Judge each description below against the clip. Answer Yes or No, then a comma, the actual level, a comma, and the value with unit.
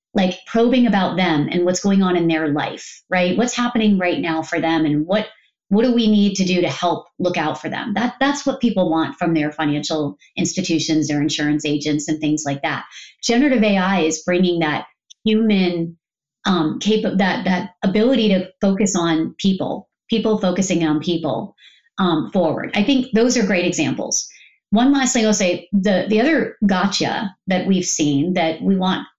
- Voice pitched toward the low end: No, medium, 185 Hz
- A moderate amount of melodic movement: Yes, average, 4.8 semitones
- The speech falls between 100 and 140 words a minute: No, average, 185 wpm